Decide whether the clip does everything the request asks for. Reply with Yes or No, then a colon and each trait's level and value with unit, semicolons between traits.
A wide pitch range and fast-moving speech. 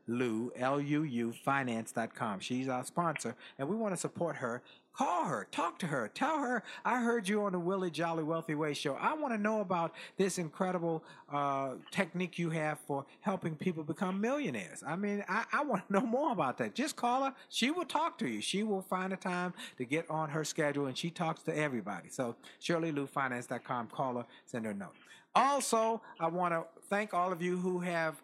Yes: wide, 6.1 semitones; fast, 210 wpm